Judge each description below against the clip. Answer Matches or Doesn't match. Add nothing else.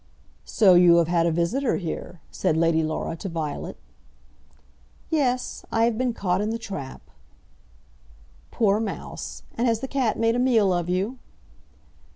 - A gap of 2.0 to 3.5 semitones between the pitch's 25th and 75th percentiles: Doesn't match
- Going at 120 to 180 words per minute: Matches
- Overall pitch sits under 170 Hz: Doesn't match